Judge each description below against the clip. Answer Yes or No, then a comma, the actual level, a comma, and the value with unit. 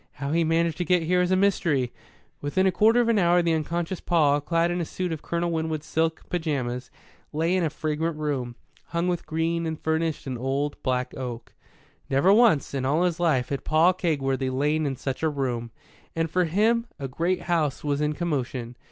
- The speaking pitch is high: No, medium, 160 Hz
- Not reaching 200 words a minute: No, fast, 205 wpm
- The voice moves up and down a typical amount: Yes, average, 3.7 semitones